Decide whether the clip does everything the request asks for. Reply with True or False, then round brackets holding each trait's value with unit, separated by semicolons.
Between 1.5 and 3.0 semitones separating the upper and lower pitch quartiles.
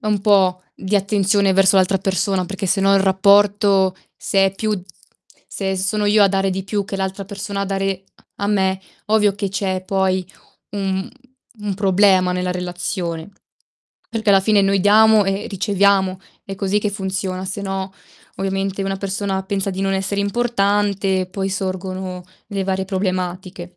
False (1.1 semitones)